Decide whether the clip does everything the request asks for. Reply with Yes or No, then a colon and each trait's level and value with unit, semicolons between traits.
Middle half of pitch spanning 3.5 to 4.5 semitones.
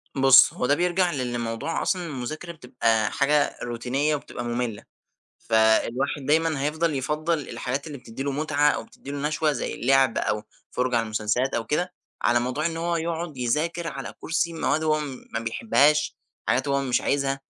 Yes: average, 4.2 semitones